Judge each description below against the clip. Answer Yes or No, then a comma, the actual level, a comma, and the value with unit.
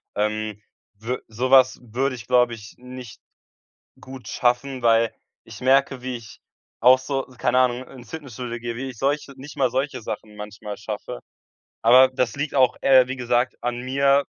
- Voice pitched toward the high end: No, low, 125 Hz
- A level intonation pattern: Yes, narrow, 2.3 semitones